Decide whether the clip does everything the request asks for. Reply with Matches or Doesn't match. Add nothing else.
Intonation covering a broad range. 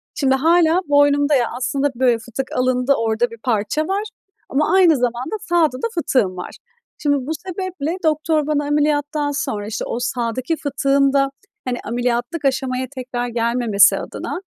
Doesn't match